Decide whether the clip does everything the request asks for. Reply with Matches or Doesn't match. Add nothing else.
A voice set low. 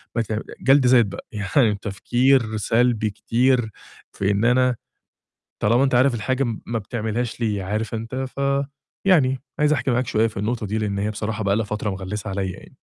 Matches